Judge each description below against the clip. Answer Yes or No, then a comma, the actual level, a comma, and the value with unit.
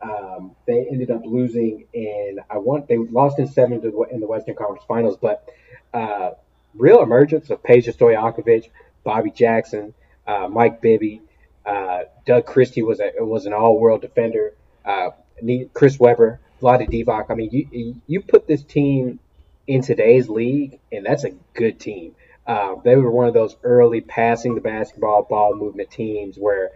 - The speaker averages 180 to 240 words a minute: No, average, 170 wpm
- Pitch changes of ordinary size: Yes, average, 3.3 semitones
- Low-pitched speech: Yes, low, 115 Hz